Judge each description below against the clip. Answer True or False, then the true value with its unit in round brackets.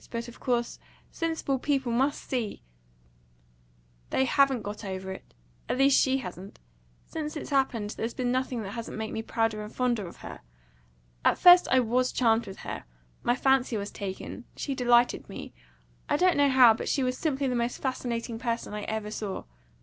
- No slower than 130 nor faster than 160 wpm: False (185 wpm)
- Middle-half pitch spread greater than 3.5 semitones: True (3.9 semitones)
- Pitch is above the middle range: True (240 Hz)